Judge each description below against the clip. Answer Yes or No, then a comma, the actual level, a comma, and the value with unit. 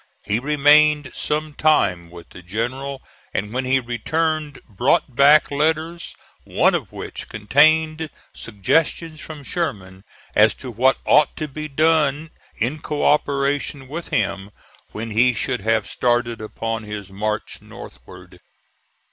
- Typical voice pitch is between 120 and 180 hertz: Yes, low, 135 Hz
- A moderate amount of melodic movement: No, wide, 5.7 semitones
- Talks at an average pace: No, slow, 130 wpm